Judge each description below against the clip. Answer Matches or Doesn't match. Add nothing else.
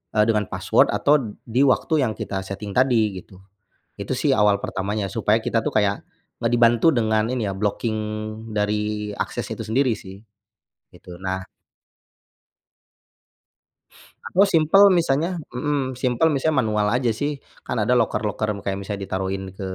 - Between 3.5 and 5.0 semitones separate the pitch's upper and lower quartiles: Matches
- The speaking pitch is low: Matches